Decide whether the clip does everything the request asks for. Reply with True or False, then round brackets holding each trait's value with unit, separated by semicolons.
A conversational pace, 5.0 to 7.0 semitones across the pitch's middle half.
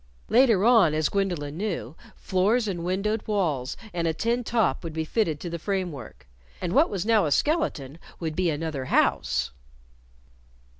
True (160 wpm; 5.5 semitones)